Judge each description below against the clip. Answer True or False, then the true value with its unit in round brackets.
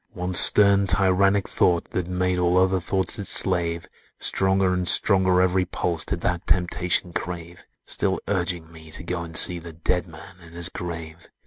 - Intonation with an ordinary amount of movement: False (1.6 semitones)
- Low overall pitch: True (90 Hz)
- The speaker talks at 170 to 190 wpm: True (175 wpm)